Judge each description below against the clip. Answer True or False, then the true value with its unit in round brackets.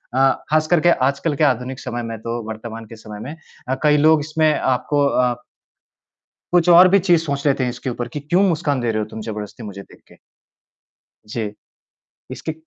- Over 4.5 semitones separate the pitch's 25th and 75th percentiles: True (5.2 semitones)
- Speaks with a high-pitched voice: False (135 Hz)